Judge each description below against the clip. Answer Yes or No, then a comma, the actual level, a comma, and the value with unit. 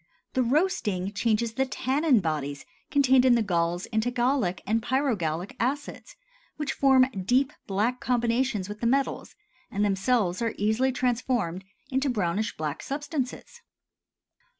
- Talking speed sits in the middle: No, slow, 130 wpm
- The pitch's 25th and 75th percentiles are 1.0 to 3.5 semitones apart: No, average, 5.0 semitones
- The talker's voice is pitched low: No, high, 235 Hz